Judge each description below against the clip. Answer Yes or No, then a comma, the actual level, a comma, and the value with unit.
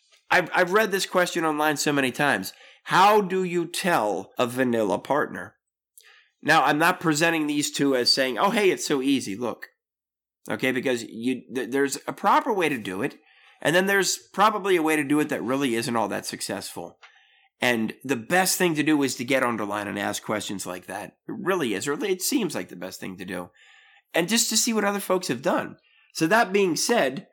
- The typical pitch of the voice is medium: Yes, medium, 155 Hz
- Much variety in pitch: Yes, wide, 7.3 semitones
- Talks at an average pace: No, fast, 215 wpm